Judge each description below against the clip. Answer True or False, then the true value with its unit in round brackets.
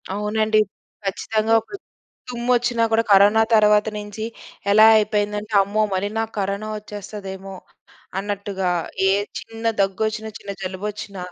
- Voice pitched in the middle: False (210 Hz)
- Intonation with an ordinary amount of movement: False (1.6 semitones)